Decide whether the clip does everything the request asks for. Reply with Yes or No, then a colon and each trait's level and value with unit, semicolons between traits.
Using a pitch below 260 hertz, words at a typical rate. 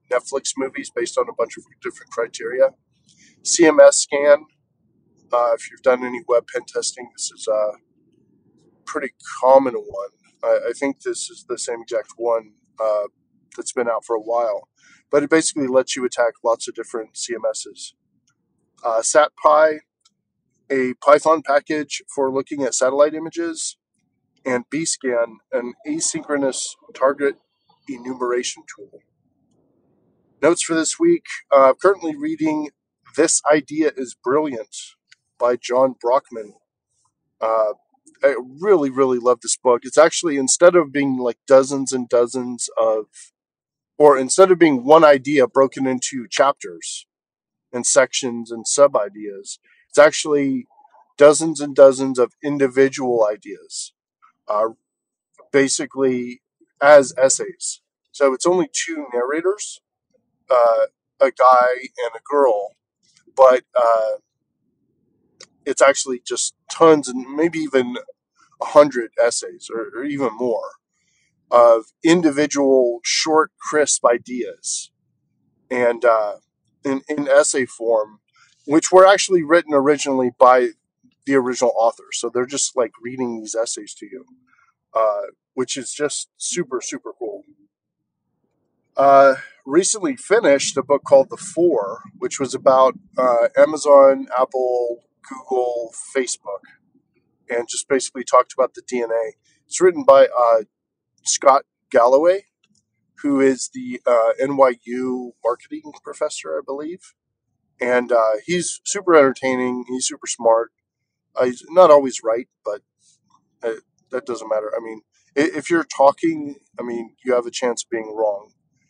No: medium, 140 Hz; slow, 130 wpm